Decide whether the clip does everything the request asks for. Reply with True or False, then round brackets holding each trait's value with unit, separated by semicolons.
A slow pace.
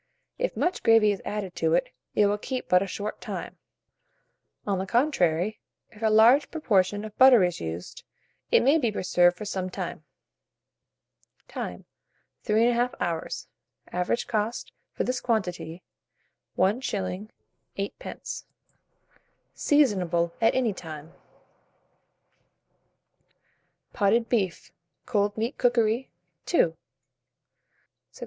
True (115 wpm)